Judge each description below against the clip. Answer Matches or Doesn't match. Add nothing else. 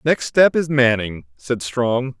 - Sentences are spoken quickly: Doesn't match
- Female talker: Doesn't match